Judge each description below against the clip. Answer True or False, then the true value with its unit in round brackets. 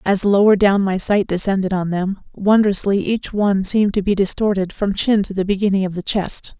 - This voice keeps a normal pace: False (210 wpm)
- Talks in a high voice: True (195 Hz)